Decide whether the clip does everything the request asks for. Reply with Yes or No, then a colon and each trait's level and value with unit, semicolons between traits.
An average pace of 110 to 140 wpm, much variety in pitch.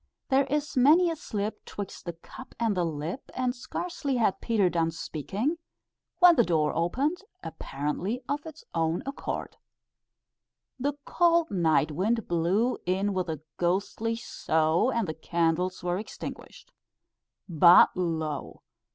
Yes: slow, 135 wpm; wide, 7.5 semitones